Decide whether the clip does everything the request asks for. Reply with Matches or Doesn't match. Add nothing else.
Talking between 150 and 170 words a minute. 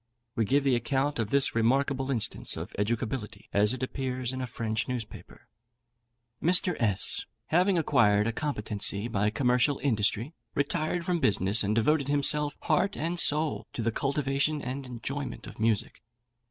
Matches